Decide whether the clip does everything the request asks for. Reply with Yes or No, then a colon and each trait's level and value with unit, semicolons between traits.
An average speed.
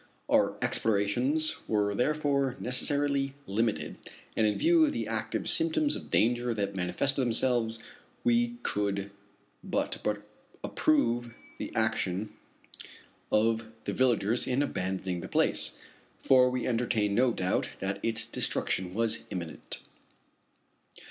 No: slow, 115 wpm